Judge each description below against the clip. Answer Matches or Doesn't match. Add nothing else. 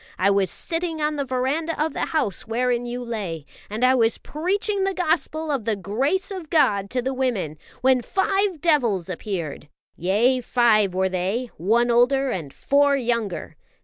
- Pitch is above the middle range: Matches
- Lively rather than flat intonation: Matches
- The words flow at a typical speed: Matches